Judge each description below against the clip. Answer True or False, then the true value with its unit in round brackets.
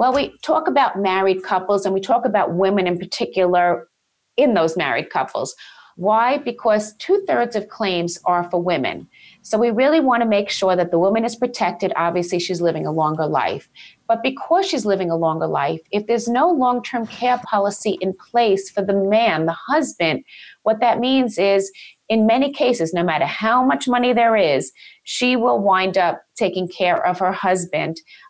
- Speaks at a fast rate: False (185 wpm)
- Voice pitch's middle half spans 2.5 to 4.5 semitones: False (5.1 semitones)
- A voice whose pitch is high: True (205 Hz)